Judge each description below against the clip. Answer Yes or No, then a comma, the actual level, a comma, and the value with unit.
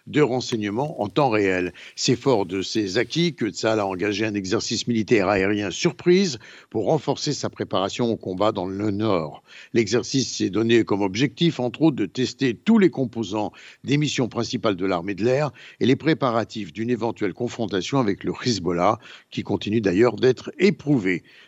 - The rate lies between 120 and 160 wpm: No, fast, 170 wpm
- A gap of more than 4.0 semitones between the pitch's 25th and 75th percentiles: Yes, average, 4.6 semitones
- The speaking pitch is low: Yes, low, 115 Hz